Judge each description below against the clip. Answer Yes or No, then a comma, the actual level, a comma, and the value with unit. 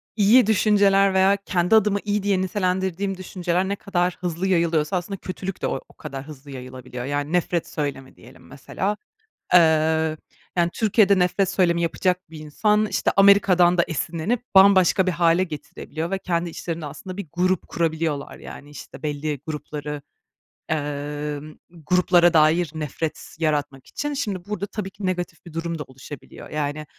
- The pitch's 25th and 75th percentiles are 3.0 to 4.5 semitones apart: Yes, average, 3.9 semitones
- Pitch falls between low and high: Yes, medium, 175 Hz